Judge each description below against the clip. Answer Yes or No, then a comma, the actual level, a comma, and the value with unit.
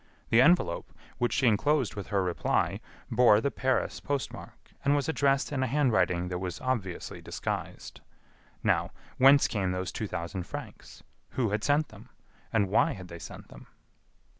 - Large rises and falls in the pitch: Yes, wide, 6.5 semitones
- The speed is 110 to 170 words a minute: Yes, average, 165 wpm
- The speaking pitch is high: No, low, 115 Hz